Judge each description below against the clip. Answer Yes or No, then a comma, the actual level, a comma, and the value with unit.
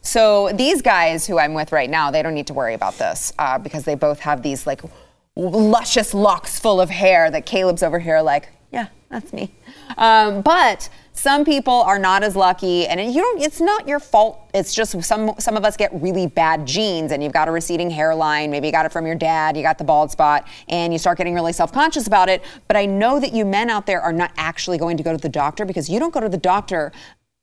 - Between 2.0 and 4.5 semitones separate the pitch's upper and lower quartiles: No, average, 5.2 semitones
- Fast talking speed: Yes, fast, 240 wpm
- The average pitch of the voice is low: No, medium, 180 Hz